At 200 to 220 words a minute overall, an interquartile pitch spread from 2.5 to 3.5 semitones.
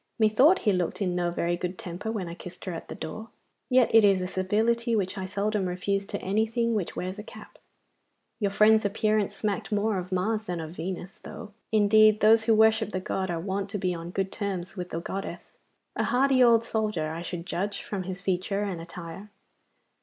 Yes: fast, 205 wpm; average, 3.1 semitones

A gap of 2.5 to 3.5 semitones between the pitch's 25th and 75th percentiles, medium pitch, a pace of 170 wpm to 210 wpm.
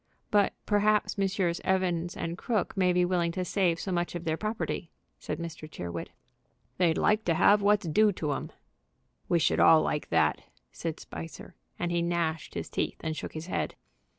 Yes: average, 3.0 semitones; medium, 175 Hz; average, 180 wpm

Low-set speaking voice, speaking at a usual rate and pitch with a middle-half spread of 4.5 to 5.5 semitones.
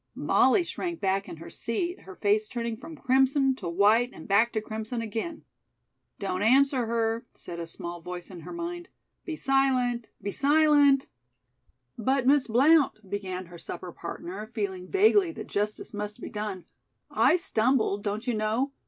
No: high, 225 Hz; average, 160 wpm; average, 5.2 semitones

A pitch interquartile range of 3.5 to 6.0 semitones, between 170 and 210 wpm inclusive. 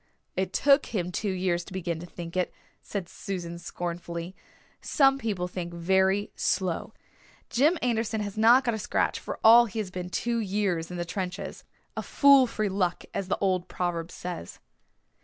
Yes: average, 3.8 semitones; average, 175 wpm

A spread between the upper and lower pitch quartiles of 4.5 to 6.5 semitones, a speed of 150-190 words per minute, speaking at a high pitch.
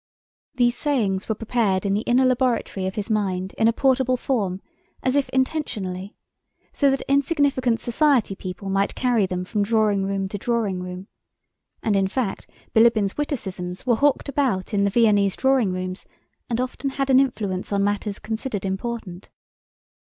Yes: average, 4.8 semitones; average, 160 wpm; high, 220 Hz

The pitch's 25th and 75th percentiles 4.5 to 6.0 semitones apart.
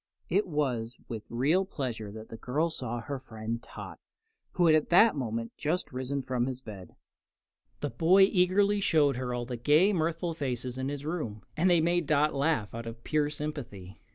Yes: wide, 5.6 semitones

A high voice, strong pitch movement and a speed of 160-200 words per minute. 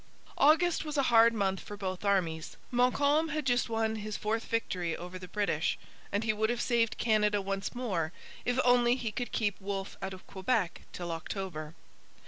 No: high, 215 Hz; average, 4.2 semitones; average, 180 wpm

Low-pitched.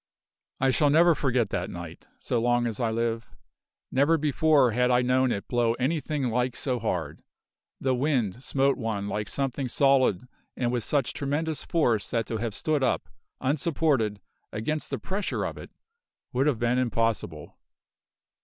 Yes: low, 125 Hz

